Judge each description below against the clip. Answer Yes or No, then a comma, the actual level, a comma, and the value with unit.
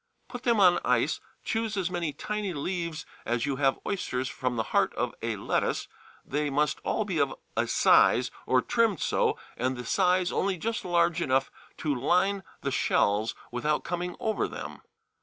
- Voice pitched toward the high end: No, medium, 170 Hz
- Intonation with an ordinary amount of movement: No, wide, 6.3 semitones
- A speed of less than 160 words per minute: No, average, 175 wpm